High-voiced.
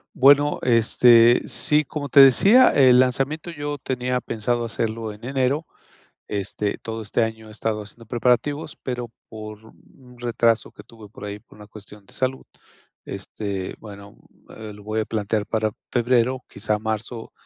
No: low, 115 Hz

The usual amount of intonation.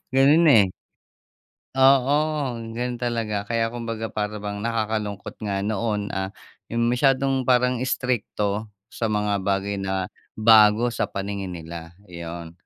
Yes: average, 3.3 semitones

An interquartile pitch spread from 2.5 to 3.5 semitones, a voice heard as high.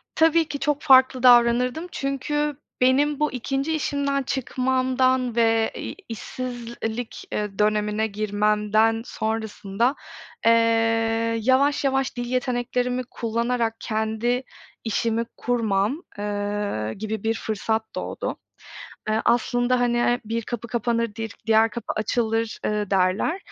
Yes: average, 2.8 semitones; high, 235 Hz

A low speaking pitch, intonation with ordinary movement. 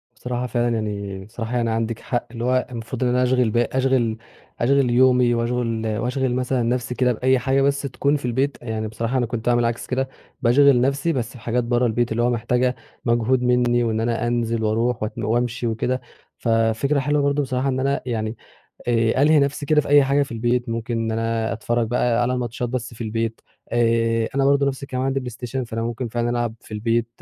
No: low, 120 Hz; narrow, 2.0 semitones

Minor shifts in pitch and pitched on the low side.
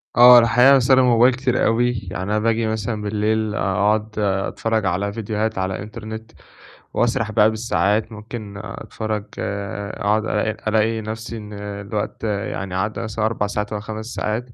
Yes: narrow, 1.7 semitones; low, 110 Hz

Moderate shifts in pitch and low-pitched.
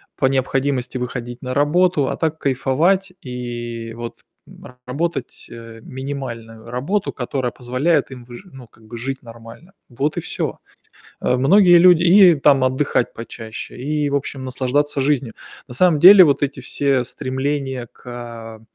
Yes: average, 3.3 semitones; low, 130 Hz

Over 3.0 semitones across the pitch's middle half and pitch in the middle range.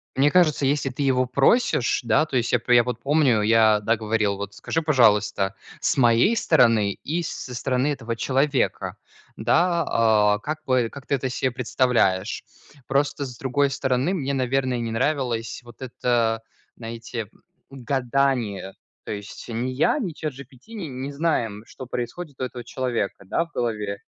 No: average, 3.5 semitones; low, 125 Hz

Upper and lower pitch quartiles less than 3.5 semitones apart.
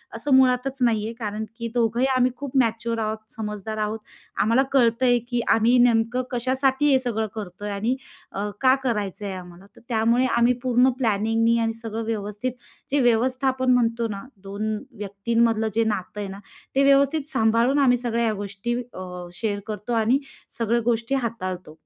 Yes: average, 2.9 semitones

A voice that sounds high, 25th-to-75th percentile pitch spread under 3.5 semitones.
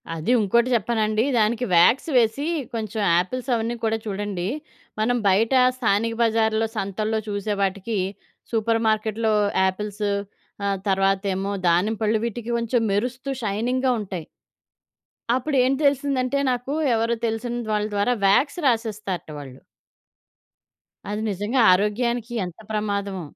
Yes: high, 220 Hz; average, 3.0 semitones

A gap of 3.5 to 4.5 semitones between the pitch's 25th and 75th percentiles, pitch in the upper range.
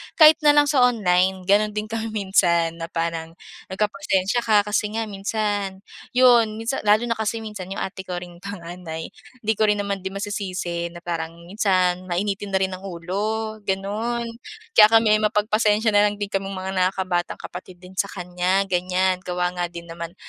No: average, 3.0 semitones; high, 195 Hz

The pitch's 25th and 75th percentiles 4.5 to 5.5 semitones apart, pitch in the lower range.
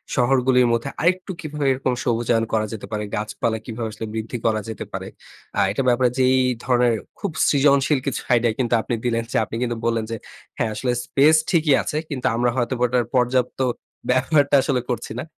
No: average, 2.8 semitones; low, 125 Hz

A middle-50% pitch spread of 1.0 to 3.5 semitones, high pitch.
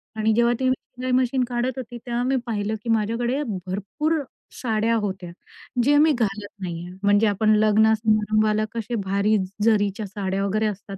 Yes: average, 2.9 semitones; high, 215 Hz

